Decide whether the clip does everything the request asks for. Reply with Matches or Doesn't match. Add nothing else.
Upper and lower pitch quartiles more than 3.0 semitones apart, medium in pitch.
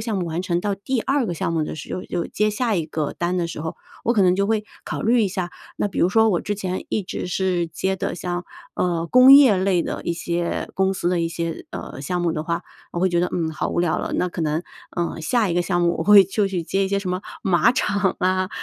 Doesn't match